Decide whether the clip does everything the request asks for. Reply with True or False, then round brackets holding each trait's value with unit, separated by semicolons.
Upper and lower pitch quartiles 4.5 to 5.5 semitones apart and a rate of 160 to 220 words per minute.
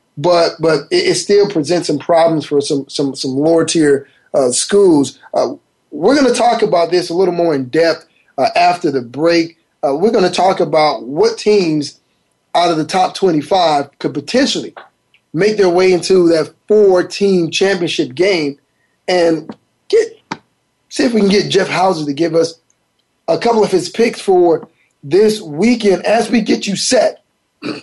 True (5.0 semitones; 175 wpm)